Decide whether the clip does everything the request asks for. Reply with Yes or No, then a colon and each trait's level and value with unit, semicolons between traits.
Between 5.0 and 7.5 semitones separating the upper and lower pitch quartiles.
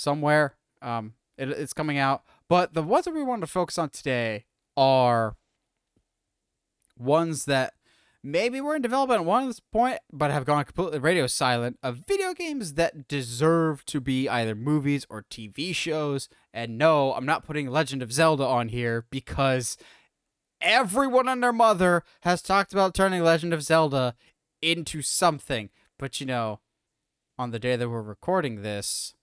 Yes: average, 5.3 semitones